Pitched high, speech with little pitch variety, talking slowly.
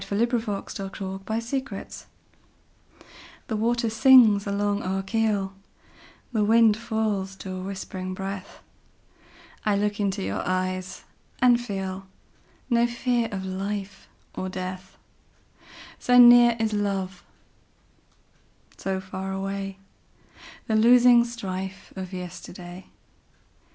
No: high, 200 Hz; average, 3.1 semitones; slow, 95 wpm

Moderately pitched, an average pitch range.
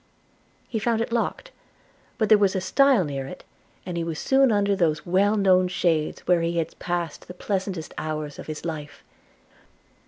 Yes: medium, 180 Hz; average, 4.1 semitones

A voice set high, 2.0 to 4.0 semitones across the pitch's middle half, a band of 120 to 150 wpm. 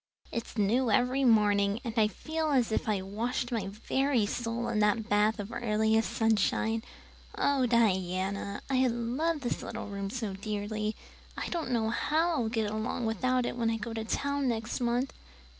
No: high, 225 Hz; average, 2.8 semitones; average, 175 wpm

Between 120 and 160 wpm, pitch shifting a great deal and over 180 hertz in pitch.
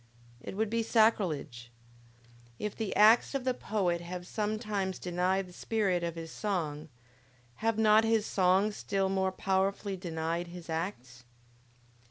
No: average, 140 wpm; average, 3.8 semitones; high, 190 Hz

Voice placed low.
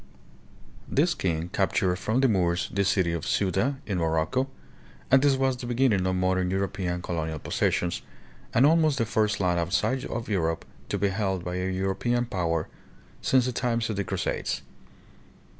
Yes: very low, 95 Hz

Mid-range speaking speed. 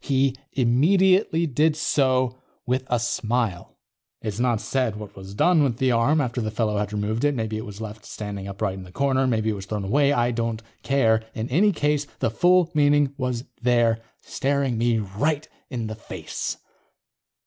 Yes: average, 180 wpm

